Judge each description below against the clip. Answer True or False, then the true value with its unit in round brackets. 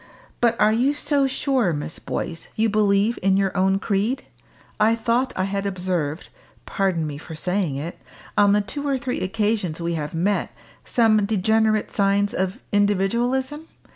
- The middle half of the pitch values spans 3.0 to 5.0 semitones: True (3.6 semitones)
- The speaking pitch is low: False (205 Hz)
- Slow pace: False (160 wpm)